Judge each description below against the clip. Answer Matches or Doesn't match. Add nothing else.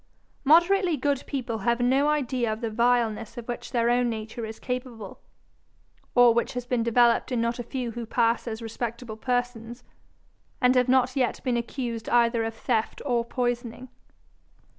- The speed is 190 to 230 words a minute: Doesn't match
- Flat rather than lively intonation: Matches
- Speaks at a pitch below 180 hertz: Doesn't match